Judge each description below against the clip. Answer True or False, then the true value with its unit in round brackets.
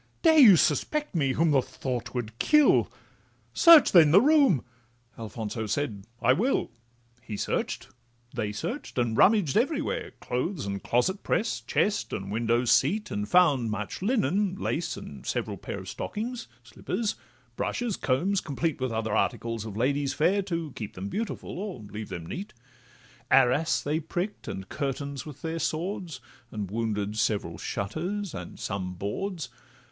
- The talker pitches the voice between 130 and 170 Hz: True (140 Hz)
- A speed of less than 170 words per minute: True (150 wpm)